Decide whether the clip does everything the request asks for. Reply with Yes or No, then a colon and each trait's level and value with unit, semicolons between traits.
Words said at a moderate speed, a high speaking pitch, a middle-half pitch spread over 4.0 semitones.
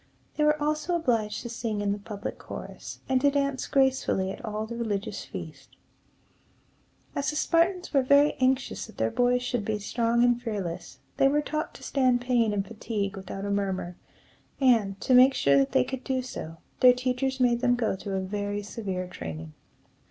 Yes: average, 190 wpm; high, 235 Hz; average, 4.7 semitones